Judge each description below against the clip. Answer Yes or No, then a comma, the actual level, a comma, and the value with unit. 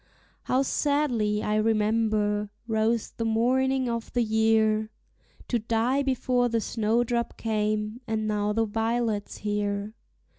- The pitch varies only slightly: Yes, narrow, 2.0 semitones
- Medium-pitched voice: No, high, 225 Hz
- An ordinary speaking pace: No, slow, 120 wpm